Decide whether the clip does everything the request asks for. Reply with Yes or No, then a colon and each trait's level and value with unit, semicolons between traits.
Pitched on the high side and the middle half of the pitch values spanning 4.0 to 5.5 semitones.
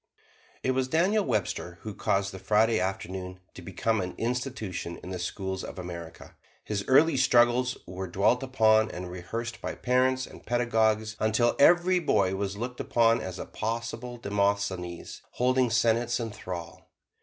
No: low, 110 Hz; average, 4.5 semitones